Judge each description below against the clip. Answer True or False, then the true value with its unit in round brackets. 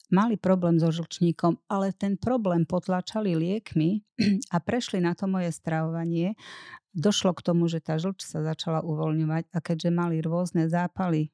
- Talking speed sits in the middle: True (155 wpm)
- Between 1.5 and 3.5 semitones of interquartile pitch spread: True (2.9 semitones)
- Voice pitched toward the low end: False (175 Hz)